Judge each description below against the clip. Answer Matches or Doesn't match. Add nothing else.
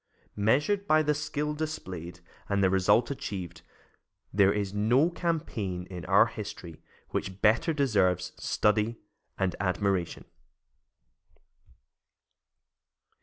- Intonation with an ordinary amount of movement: Doesn't match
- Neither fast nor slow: Doesn't match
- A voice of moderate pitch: Doesn't match